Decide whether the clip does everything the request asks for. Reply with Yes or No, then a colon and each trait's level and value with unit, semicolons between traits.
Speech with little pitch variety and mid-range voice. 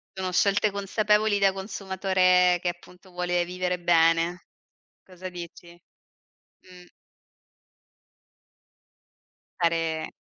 Yes: narrow, 1.6 semitones; medium, 180 Hz